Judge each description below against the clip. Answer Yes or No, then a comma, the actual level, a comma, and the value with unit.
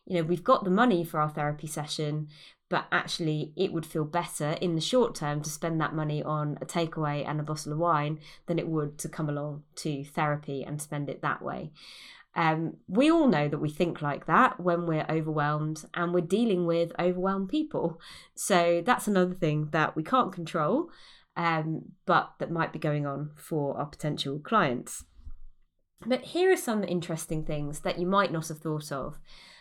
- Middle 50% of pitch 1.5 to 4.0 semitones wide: Yes, average, 2.9 semitones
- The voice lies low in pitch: No, medium, 160 Hz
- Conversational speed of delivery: Yes, average, 195 wpm